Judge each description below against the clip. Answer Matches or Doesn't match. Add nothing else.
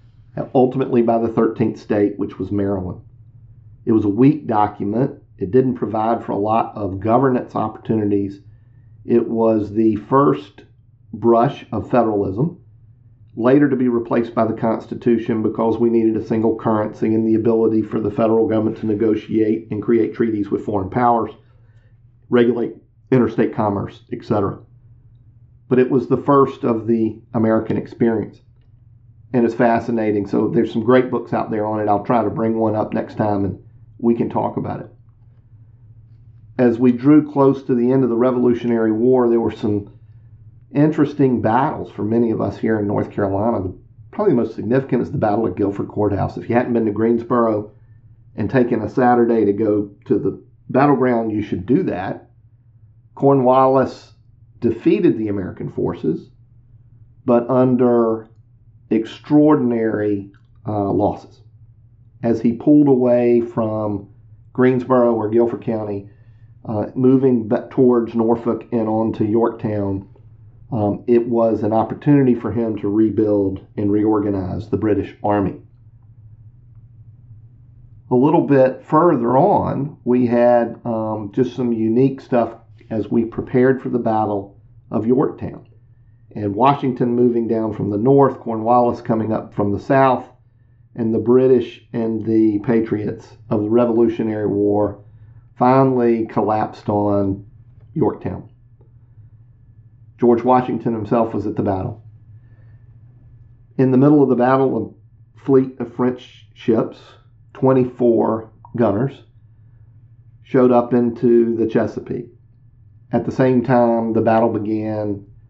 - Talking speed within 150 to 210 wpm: Doesn't match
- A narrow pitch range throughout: Matches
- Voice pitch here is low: Matches